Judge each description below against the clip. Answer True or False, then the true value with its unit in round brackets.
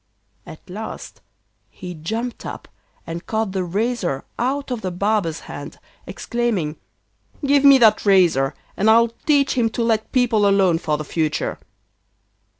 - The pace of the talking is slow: False (145 wpm)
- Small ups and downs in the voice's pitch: False (5.5 semitones)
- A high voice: True (210 Hz)